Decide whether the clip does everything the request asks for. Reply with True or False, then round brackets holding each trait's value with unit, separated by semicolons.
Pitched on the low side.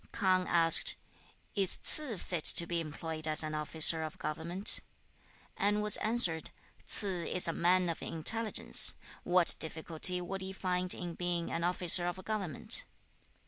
False (175 Hz)